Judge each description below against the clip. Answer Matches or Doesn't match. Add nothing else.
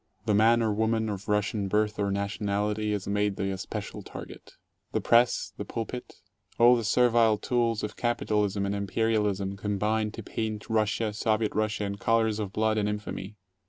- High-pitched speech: Doesn't match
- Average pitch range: Doesn't match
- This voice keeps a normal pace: Matches